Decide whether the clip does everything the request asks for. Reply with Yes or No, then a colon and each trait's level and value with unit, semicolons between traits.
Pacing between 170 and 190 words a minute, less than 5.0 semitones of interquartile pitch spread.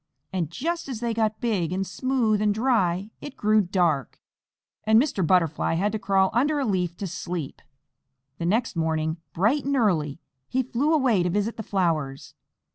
No: average, 175 wpm; average, 5.3 semitones